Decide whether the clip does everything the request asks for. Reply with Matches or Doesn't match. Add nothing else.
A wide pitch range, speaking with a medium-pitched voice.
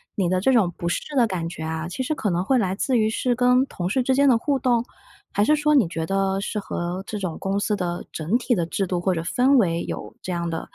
Doesn't match